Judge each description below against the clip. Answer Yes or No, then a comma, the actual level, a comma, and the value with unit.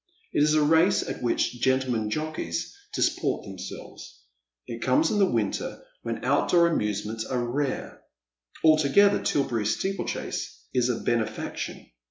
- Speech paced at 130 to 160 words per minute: Yes, slow, 135 wpm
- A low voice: Yes, low, 130 Hz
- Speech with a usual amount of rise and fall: No, wide, 5.9 semitones